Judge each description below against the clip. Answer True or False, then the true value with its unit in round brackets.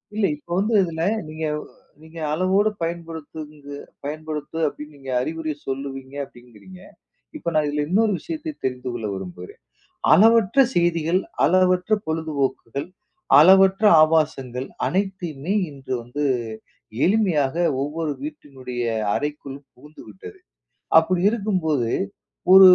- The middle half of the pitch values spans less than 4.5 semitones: False (4.8 semitones)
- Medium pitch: True (155 Hz)